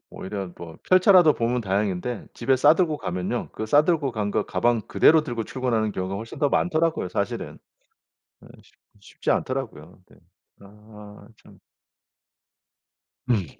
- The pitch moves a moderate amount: No, wide, 6.2 semitones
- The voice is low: Yes, low, 115 Hz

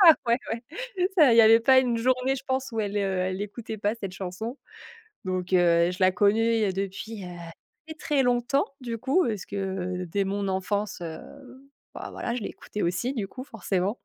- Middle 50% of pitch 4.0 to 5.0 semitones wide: Yes, average, 4.3 semitones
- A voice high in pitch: Yes, high, 210 Hz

